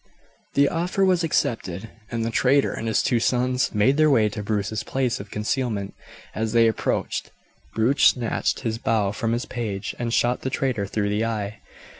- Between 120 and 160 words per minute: No, average, 180 wpm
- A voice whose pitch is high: No, low, 115 Hz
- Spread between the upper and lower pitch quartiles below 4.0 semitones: Yes, average, 3.3 semitones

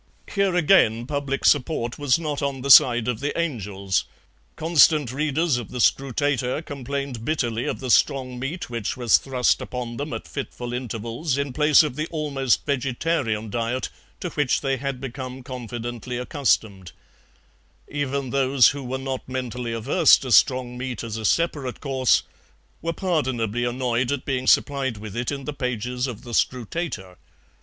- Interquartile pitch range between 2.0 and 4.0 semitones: Yes, average, 2.9 semitones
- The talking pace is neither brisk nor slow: Yes, average, 160 wpm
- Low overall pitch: Yes, low, 130 Hz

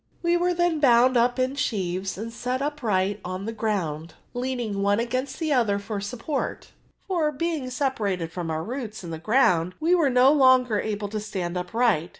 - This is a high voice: Yes, high, 230 Hz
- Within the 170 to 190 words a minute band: Yes, average, 180 wpm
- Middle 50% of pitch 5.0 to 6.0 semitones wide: Yes, average, 5.3 semitones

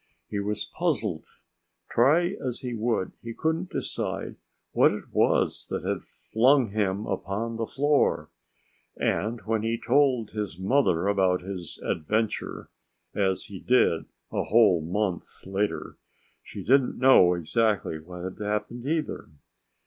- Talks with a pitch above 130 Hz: No, low, 110 Hz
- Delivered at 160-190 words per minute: No, slow, 135 wpm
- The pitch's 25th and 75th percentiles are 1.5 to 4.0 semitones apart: No, average, 4.6 semitones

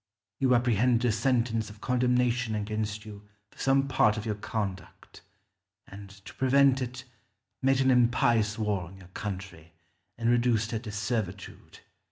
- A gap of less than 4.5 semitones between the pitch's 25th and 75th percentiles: Yes, average, 3.2 semitones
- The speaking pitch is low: Yes, low, 110 Hz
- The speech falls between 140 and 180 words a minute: Yes, average, 150 wpm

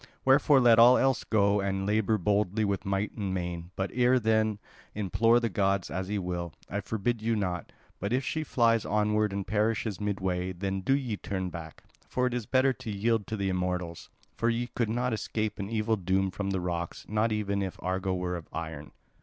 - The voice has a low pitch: Yes, low, 105 Hz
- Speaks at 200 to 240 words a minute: Yes, fast, 205 wpm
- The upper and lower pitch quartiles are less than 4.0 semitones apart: Yes, average, 3.3 semitones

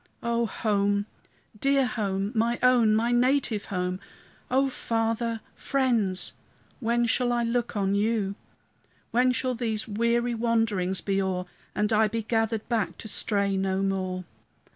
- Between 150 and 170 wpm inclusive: No, average, 140 wpm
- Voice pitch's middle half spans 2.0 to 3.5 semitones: Yes, average, 2.9 semitones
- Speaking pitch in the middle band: No, high, 225 Hz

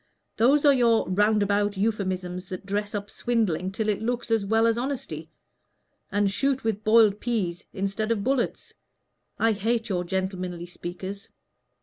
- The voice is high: Yes, high, 205 Hz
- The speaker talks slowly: No, average, 145 wpm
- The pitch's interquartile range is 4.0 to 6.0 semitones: No, average, 3.2 semitones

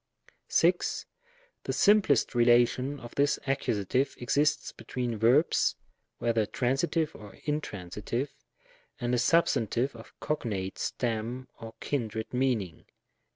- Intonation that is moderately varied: Yes, average, 3.8 semitones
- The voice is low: Yes, low, 120 Hz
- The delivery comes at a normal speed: No, slow, 110 wpm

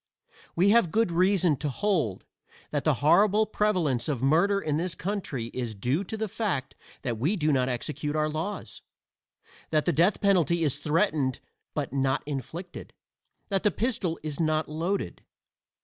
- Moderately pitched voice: Yes, medium, 160 Hz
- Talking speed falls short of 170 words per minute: Yes, average, 160 wpm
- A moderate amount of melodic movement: No, wide, 5.7 semitones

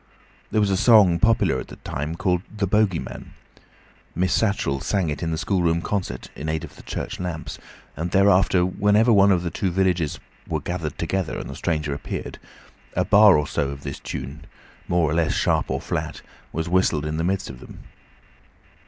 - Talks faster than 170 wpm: Yes, average, 195 wpm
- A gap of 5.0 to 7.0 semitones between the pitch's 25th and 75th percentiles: No, average, 3.8 semitones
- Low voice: Yes, very low, 90 Hz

